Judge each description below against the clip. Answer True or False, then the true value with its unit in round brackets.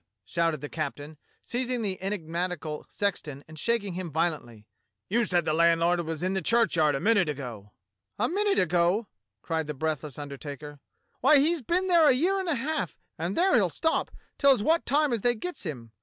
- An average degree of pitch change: False (7.9 semitones)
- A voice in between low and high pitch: True (175 Hz)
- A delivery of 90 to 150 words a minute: False (185 wpm)